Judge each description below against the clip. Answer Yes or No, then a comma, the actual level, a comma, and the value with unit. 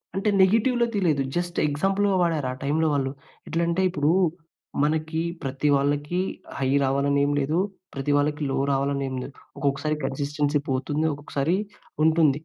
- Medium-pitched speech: Yes, medium, 145 Hz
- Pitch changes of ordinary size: Yes, average, 3.1 semitones